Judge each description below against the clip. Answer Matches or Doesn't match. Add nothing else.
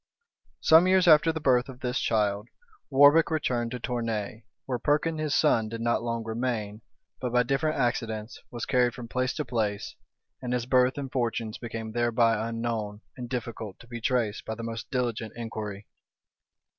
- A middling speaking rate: Matches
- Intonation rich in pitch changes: Doesn't match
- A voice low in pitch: Matches